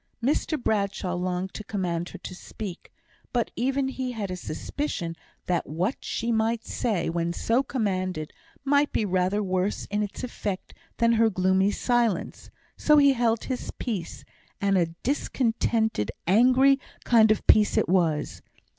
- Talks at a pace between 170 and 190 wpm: No, average, 150 wpm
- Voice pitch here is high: Yes, high, 210 Hz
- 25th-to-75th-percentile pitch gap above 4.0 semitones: Yes, average, 4.7 semitones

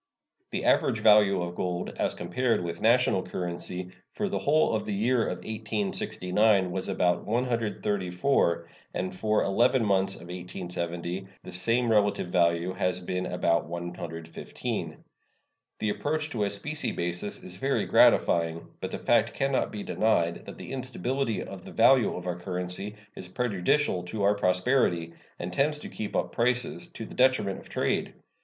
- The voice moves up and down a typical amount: Yes, average, 4.8 semitones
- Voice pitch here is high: No, low, 100 Hz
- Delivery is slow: No, average, 160 wpm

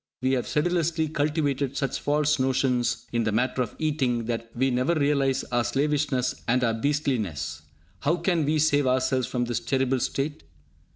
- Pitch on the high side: No, low, 135 Hz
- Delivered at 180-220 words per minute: No, average, 165 wpm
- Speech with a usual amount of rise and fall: Yes, average, 3.2 semitones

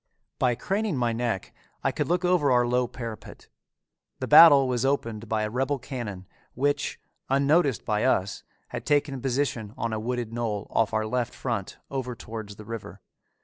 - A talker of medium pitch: No, low, 120 Hz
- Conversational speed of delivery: Yes, average, 170 wpm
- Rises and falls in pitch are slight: No, average, 3.8 semitones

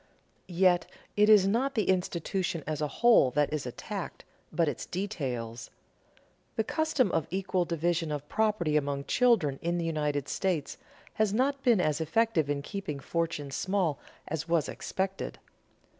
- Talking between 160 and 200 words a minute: No, average, 150 wpm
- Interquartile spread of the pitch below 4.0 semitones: No, average, 5.2 semitones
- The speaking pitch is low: No, medium, 170 Hz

